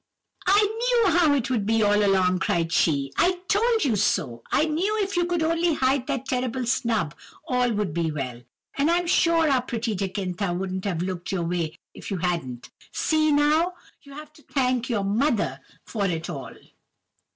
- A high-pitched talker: Yes, high, 235 Hz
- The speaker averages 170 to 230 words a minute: Yes, average, 185 wpm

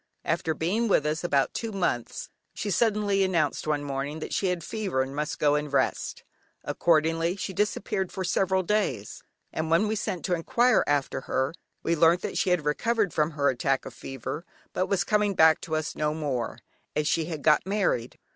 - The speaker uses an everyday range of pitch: Yes, average, 4.5 semitones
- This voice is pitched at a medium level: Yes, medium, 165 Hz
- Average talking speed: Yes, average, 195 wpm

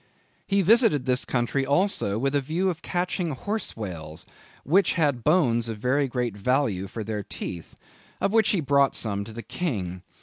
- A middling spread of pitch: No, wide, 7.8 semitones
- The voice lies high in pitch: No, low, 135 Hz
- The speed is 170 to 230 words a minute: Yes, average, 175 wpm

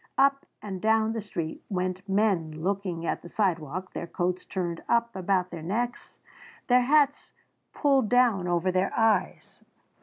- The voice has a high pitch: Yes, high, 195 Hz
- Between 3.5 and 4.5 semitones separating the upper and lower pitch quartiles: Yes, average, 4.2 semitones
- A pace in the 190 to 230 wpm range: No, average, 150 wpm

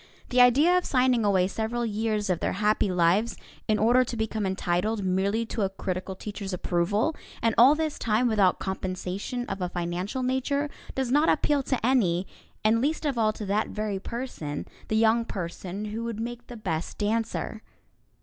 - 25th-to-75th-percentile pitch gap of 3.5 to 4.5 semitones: Yes, average, 4.2 semitones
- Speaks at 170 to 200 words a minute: Yes, average, 180 wpm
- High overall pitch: Yes, high, 215 Hz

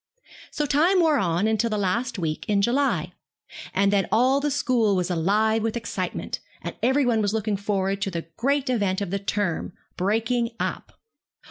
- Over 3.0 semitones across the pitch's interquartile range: Yes, average, 4.1 semitones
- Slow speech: No, average, 185 wpm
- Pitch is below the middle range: No, high, 215 Hz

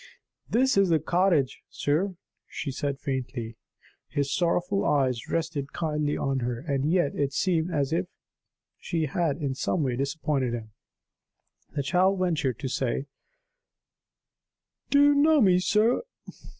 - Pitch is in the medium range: Yes, medium, 150 Hz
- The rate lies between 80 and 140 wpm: Yes, slow, 135 wpm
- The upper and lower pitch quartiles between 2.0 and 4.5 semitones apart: No, average, 5.0 semitones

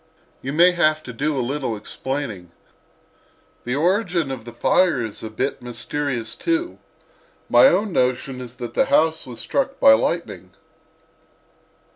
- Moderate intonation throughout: No, wide, 5.9 semitones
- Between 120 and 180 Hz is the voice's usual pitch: Yes, low, 135 Hz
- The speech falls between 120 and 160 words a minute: Yes, average, 145 wpm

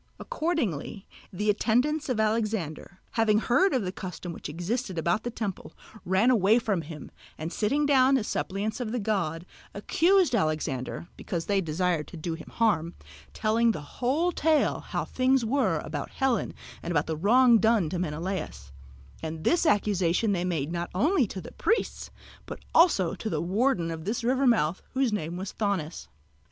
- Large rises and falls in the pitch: Yes, wide, 6.2 semitones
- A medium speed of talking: Yes, average, 170 wpm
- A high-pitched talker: Yes, high, 205 Hz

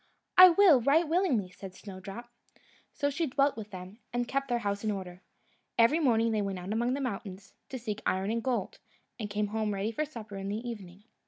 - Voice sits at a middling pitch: No, high, 220 Hz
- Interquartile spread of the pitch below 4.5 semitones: No, average, 4.8 semitones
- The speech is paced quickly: Yes, fast, 210 wpm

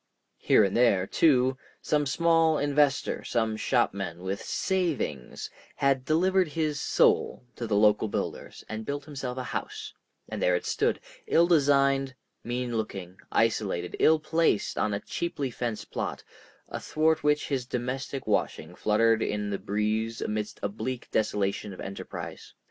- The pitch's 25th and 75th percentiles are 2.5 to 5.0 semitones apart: No, wide, 5.6 semitones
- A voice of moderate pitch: No, low, 125 Hz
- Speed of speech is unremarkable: Yes, average, 145 wpm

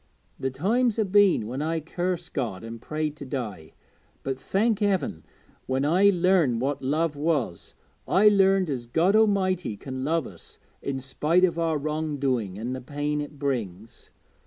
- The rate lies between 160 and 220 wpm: Yes, average, 165 wpm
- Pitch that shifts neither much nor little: No, wide, 5.8 semitones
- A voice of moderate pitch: Yes, medium, 150 Hz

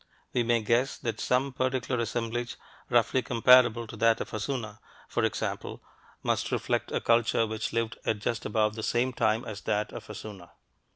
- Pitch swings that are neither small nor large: No, narrow, 2.0 semitones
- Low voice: Yes, low, 115 Hz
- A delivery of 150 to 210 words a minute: Yes, average, 170 wpm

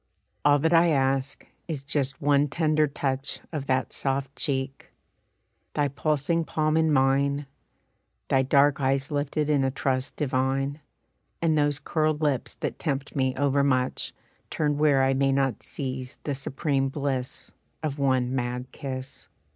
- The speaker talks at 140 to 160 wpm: Yes, average, 145 wpm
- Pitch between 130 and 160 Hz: Yes, medium, 140 Hz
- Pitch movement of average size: No, narrow, 1.8 semitones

